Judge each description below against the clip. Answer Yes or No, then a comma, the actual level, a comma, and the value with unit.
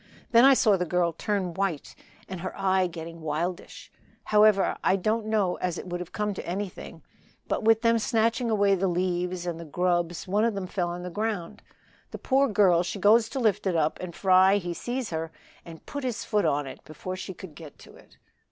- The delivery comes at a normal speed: No, fast, 215 wpm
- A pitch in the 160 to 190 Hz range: Yes, medium, 185 Hz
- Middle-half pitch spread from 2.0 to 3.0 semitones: No, average, 3.5 semitones